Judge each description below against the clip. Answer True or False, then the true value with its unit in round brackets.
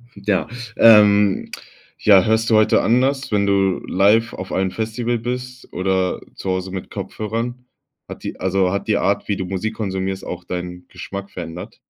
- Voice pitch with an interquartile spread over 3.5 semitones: False (2.9 semitones)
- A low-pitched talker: True (100 Hz)